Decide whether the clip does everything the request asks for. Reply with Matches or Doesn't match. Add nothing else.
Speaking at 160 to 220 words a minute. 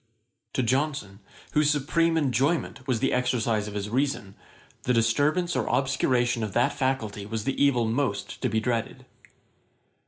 Doesn't match